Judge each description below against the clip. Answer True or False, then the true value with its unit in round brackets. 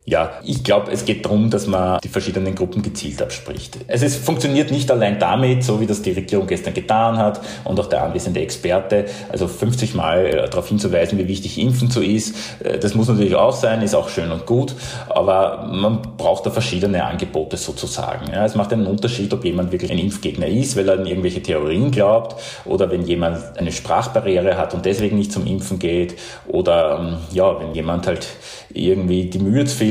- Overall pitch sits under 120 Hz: True (105 Hz)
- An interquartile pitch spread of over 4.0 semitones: False (3.4 semitones)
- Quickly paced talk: True (195 wpm)